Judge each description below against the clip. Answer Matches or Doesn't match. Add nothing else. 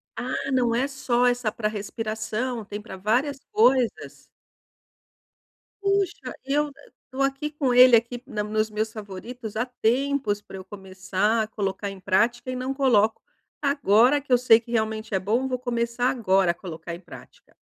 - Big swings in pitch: Doesn't match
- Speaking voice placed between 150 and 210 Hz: Doesn't match